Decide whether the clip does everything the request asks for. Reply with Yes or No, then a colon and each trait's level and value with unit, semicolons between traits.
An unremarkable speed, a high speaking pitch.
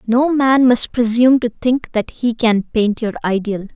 Yes: average, 190 wpm; high, 235 Hz